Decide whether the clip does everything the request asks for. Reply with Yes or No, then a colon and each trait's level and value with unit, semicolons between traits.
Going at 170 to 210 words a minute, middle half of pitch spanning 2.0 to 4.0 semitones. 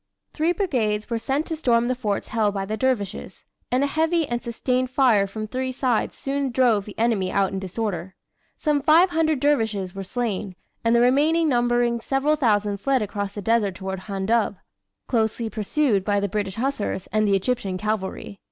No: average, 180 wpm; average, 4.5 semitones